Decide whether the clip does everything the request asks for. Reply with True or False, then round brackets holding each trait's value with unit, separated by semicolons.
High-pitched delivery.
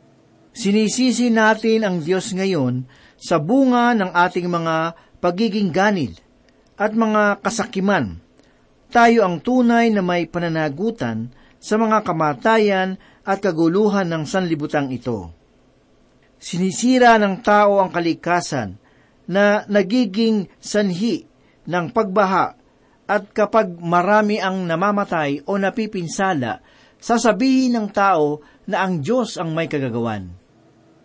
True (195 Hz)